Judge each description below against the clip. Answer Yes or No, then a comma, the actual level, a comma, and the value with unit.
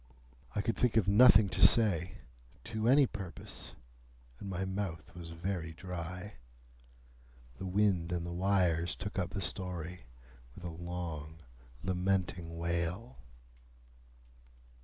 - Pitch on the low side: Yes, very low, 90 Hz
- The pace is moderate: No, slow, 120 wpm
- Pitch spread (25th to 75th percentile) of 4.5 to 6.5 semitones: No, average, 2.8 semitones